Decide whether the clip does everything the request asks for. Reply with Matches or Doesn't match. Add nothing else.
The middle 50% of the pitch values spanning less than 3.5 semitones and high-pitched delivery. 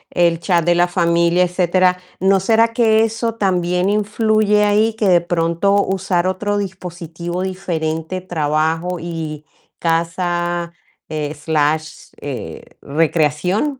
Doesn't match